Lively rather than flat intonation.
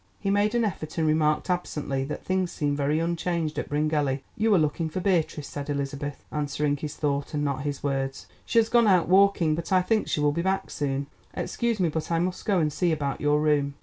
No: average, 3.8 semitones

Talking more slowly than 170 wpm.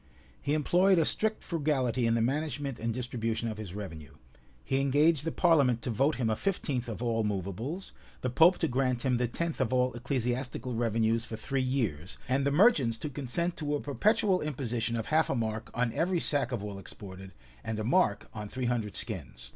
No: average, 200 wpm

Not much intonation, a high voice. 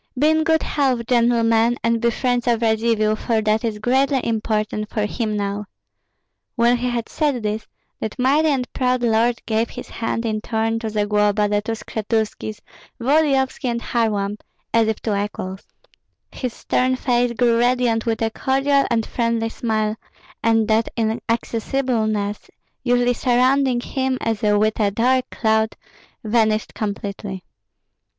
Yes: narrow, 2.3 semitones; high, 230 Hz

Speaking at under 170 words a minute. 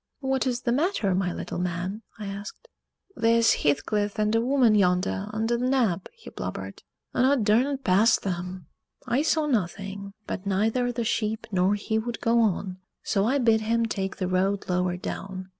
No: average, 175 wpm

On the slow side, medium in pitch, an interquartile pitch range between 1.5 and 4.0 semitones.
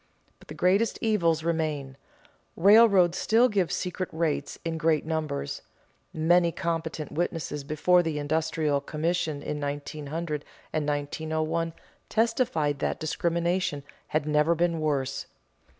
Yes: slow, 120 wpm; medium, 160 Hz; narrow, 2.5 semitones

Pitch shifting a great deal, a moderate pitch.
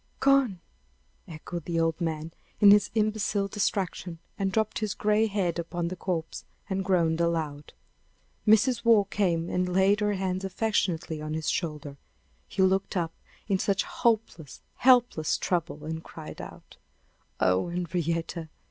No: average, 4.0 semitones; medium, 180 Hz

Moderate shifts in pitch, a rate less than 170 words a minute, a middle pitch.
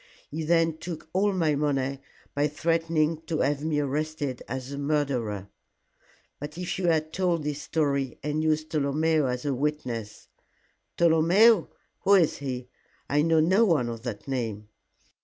Yes: average, 3.0 semitones; average, 160 wpm; medium, 150 Hz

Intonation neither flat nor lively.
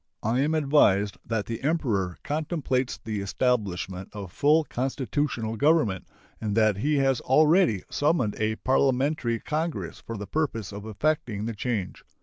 No: wide, 6.0 semitones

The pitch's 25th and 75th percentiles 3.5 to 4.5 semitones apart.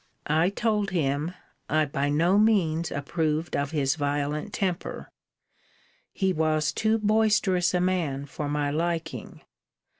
Yes: average, 4.1 semitones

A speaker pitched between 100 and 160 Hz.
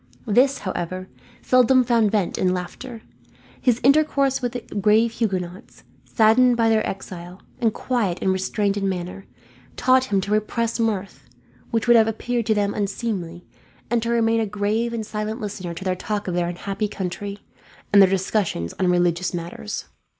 No: high, 210 Hz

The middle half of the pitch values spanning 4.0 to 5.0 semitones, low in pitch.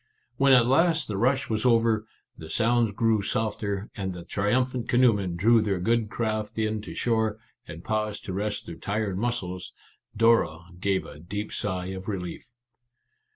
No: average, 3.2 semitones; low, 105 Hz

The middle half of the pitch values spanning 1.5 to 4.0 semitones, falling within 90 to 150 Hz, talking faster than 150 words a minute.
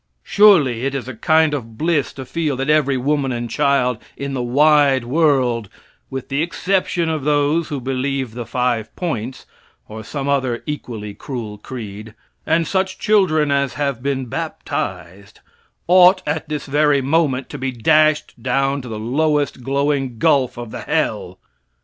Yes: average, 3.6 semitones; medium, 140 Hz; average, 160 wpm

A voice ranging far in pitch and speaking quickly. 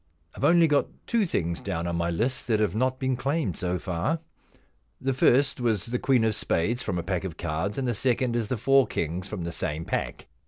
Yes: wide, 6.9 semitones; fast, 225 wpm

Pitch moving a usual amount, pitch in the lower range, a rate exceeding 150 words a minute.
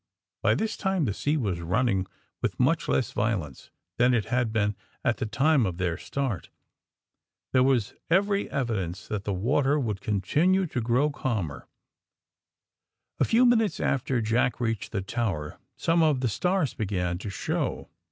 No: wide, 6.6 semitones; low, 120 Hz; average, 160 wpm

